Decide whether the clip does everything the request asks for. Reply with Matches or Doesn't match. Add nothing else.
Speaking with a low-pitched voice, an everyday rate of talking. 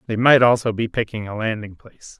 Doesn't match